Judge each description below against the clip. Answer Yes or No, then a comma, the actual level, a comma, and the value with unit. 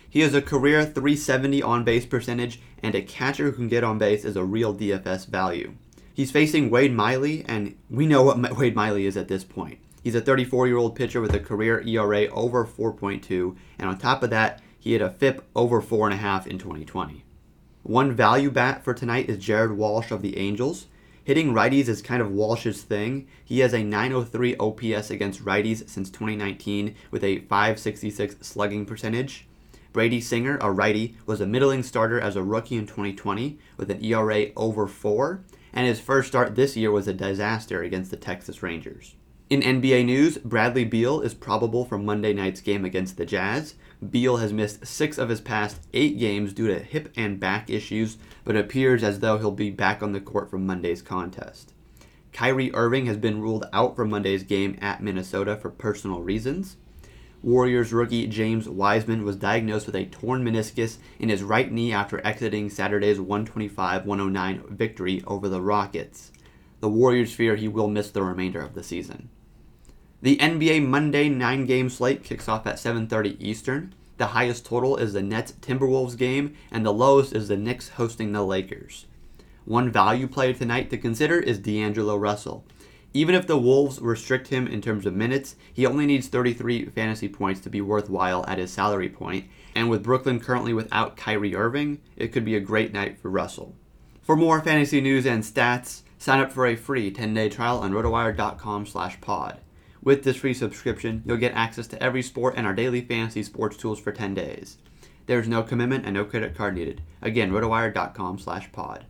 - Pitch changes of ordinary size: Yes, average, 3.6 semitones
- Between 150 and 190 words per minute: Yes, average, 185 wpm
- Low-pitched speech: Yes, low, 110 Hz